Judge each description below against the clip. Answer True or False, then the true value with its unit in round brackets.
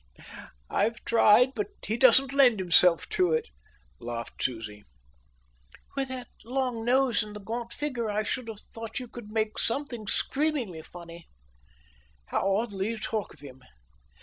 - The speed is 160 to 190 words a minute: False (150 wpm)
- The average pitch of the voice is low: False (225 Hz)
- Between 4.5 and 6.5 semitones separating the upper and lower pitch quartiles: True (4.8 semitones)